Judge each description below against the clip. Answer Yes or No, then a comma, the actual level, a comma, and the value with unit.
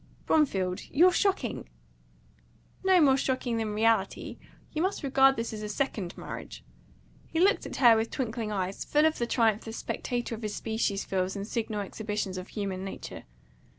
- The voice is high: Yes, high, 225 Hz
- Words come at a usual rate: Yes, average, 170 wpm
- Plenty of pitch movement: No, average, 4.8 semitones